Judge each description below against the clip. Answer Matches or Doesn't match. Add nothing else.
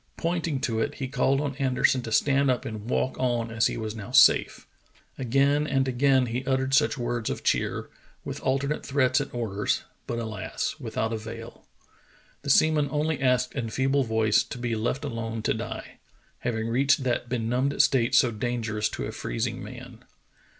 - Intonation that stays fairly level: Doesn't match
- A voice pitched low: Matches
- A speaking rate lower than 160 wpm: Doesn't match